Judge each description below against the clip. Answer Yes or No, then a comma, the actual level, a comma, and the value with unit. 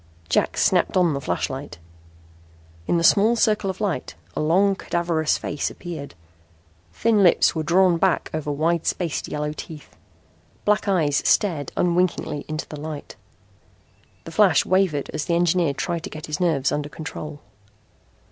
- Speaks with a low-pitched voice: No, medium, 160 Hz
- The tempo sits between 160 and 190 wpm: No, average, 150 wpm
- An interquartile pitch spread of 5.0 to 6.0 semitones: No, average, 3.7 semitones